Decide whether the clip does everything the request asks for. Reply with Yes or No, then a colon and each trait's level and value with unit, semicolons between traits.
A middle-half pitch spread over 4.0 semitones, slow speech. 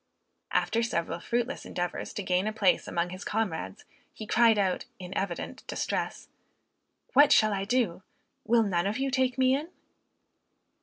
No: average, 4.6 semitones; average, 155 wpm